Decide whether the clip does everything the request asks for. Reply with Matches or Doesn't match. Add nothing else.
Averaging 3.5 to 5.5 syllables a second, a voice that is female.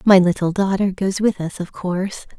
Matches